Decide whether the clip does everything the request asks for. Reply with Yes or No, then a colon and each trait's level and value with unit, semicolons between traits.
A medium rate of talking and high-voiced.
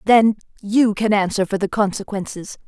Yes: average, 155 wpm; high, 205 Hz